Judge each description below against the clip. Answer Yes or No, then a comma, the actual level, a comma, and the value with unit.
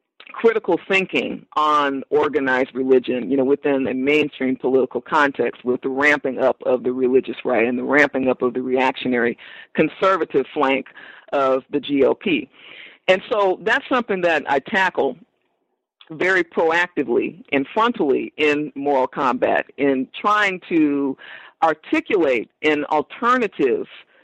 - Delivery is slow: Yes, slow, 130 wpm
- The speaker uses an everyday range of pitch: No, wide, 6.5 semitones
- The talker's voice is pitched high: No, medium, 150 Hz